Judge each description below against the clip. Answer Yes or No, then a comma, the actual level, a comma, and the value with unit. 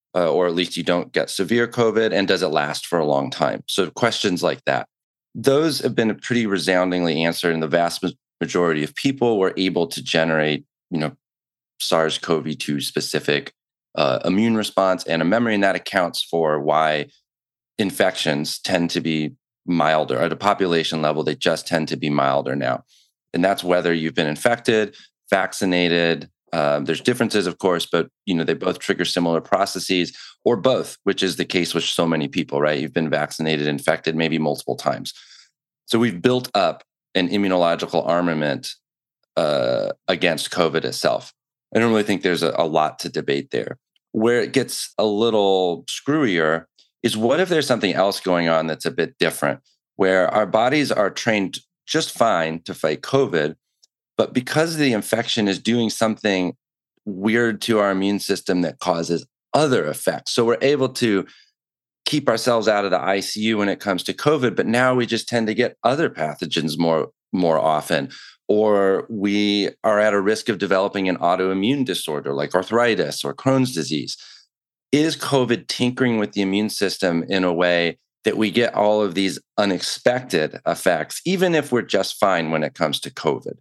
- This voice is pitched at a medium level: No, very low, 95 Hz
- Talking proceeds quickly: No, average, 175 wpm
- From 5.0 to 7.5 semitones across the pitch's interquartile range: Yes, wide, 5.5 semitones